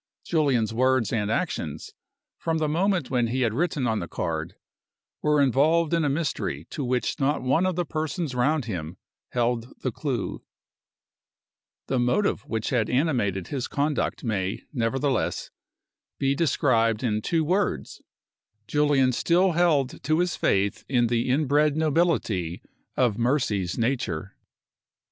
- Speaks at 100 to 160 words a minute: Yes, average, 140 wpm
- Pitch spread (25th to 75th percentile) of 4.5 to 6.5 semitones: Yes, average, 5.1 semitones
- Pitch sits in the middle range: No, low, 130 Hz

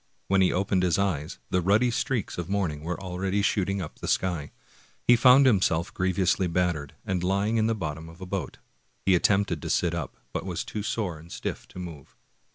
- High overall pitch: No, very low, 95 Hz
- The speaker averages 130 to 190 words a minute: No, fast, 205 wpm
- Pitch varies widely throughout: No, average, 2.9 semitones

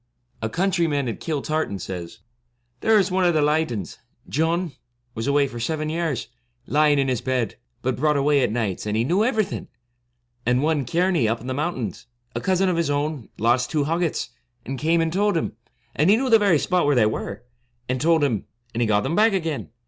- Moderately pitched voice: Yes, medium, 145 Hz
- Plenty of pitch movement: Yes, wide, 5.7 semitones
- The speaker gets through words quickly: Yes, fast, 215 wpm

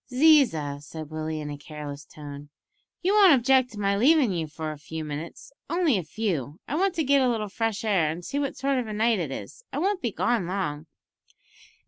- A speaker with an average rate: No, fast, 215 wpm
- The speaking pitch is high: Yes, high, 200 Hz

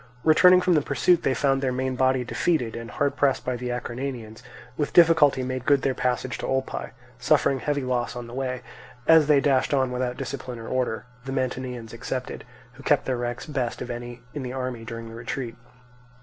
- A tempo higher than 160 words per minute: Yes, average, 200 wpm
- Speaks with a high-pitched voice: No, low, 130 Hz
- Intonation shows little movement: Yes, narrow, 2.2 semitones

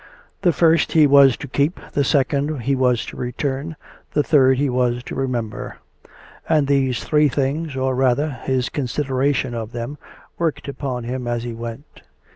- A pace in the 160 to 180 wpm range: Yes, average, 165 wpm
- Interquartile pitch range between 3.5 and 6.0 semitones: No, average, 2.7 semitones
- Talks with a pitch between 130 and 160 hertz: Yes, low, 135 Hz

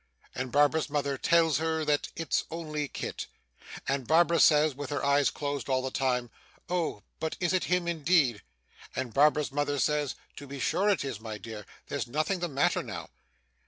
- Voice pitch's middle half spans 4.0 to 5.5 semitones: No, average, 3.1 semitones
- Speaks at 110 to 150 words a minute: No, average, 180 wpm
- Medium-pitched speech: Yes, medium, 145 Hz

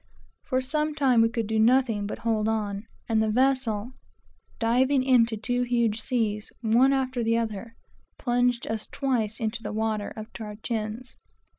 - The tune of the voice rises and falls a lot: No, narrow, 2.6 semitones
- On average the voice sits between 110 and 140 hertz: No, high, 230 Hz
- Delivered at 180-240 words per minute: No, average, 165 wpm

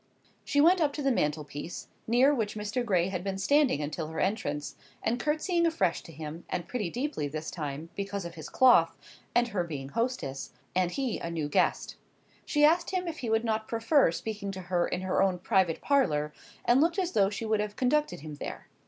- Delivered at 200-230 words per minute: Yes, fast, 205 wpm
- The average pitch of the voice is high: Yes, high, 205 Hz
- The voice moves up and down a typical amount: No, wide, 7.6 semitones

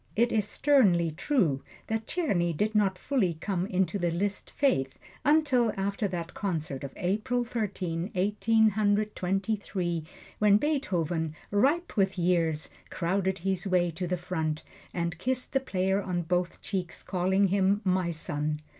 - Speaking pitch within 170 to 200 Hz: Yes, high, 190 Hz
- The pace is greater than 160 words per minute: No, average, 150 wpm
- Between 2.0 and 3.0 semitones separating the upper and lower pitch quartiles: No, average, 3.7 semitones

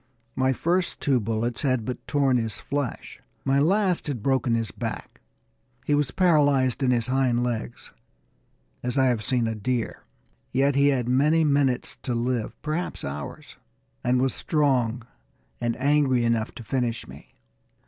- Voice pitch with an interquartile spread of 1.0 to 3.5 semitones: Yes, average, 3.1 semitones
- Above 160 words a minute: No, average, 155 wpm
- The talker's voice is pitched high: No, low, 130 Hz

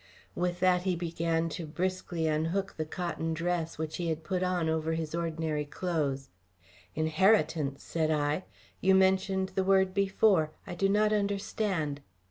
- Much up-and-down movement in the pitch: No, average, 3.0 semitones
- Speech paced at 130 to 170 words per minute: Yes, average, 150 wpm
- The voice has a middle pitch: Yes, medium, 170 Hz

